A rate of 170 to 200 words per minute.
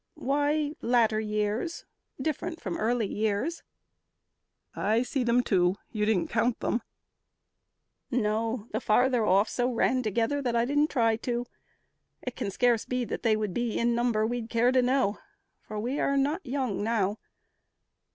No: average, 155 wpm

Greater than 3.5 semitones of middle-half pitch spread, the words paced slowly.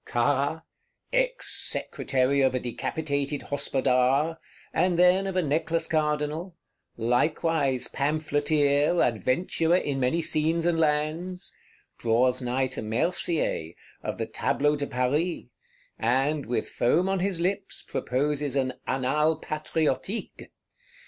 Yes: average, 4.0 semitones; slow, 110 wpm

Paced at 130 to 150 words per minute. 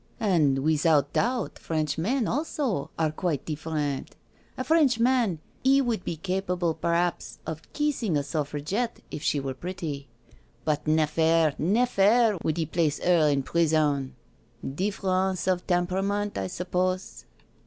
Yes: average, 145 wpm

